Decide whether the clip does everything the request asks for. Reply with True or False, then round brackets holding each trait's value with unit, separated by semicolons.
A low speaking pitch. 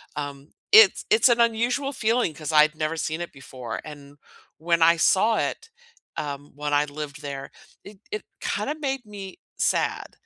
False (160 Hz)